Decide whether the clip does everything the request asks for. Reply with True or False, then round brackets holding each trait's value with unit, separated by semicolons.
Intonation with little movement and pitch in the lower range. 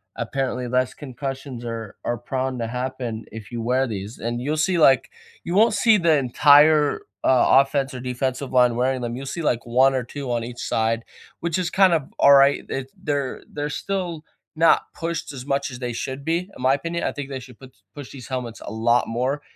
False (3.1 semitones; 130 Hz)